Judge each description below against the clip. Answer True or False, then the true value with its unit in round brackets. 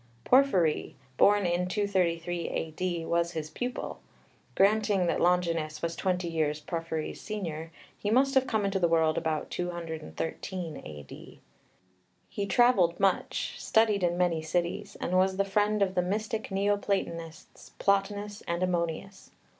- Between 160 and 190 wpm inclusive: False (135 wpm)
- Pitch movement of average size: True (3.4 semitones)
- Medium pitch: True (180 Hz)